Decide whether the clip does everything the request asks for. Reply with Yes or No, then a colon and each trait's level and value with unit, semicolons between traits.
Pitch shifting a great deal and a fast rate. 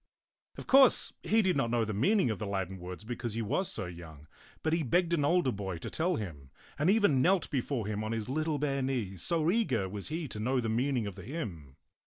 Yes: wide, 7.8 semitones; fast, 240 wpm